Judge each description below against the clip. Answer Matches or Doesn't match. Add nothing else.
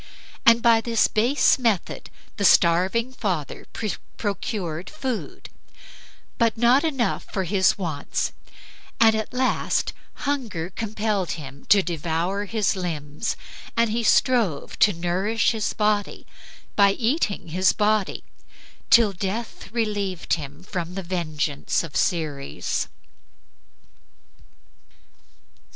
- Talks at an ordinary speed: Doesn't match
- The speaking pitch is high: Matches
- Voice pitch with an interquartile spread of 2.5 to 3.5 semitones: Doesn't match